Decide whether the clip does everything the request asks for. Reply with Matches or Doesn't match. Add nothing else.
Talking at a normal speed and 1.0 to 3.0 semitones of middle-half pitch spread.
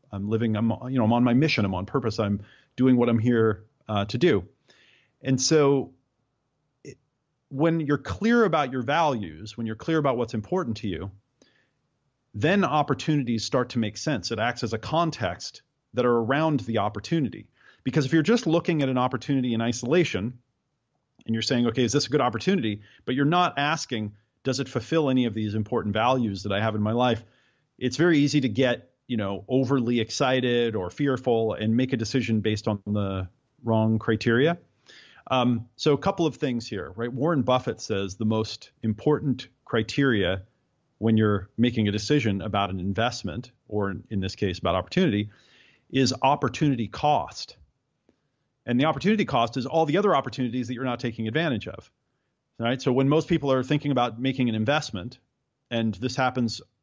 Doesn't match